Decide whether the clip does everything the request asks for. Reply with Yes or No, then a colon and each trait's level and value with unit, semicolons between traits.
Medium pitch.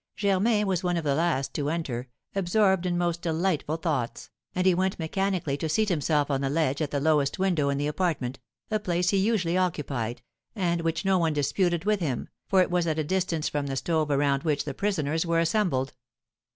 Yes: medium, 165 Hz